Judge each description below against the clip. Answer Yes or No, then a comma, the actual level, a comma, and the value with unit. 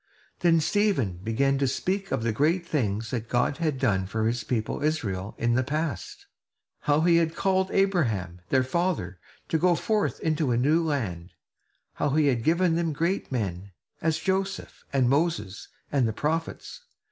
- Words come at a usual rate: Yes, average, 170 wpm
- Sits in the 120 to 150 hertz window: Yes, medium, 140 Hz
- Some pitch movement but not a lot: No, wide, 6.8 semitones